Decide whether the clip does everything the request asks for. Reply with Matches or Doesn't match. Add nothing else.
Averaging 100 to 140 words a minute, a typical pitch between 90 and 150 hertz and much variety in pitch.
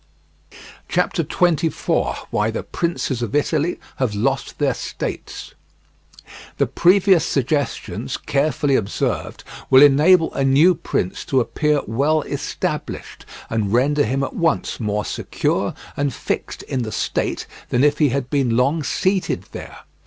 Doesn't match